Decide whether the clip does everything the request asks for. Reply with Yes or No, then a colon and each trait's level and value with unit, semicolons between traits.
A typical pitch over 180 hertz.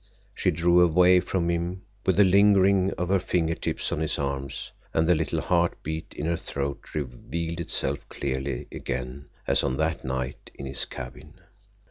No: very low, 80 Hz